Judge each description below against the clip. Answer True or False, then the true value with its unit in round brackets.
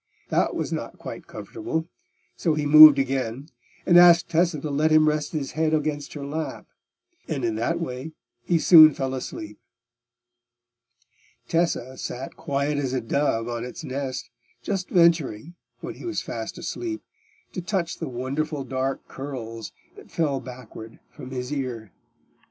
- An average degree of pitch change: True (3.9 semitones)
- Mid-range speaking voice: True (145 Hz)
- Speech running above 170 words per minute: False (150 wpm)